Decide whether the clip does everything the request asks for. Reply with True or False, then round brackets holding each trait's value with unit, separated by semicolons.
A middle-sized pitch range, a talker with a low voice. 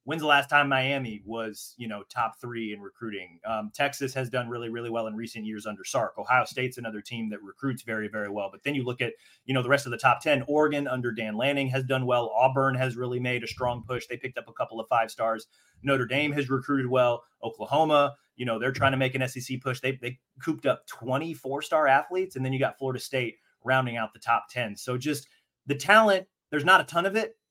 True (3.2 semitones; 130 Hz)